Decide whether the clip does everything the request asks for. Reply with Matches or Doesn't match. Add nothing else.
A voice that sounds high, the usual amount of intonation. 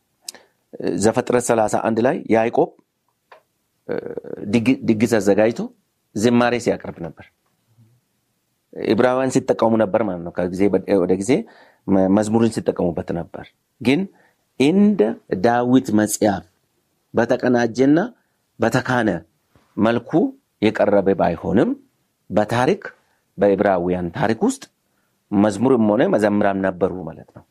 Doesn't match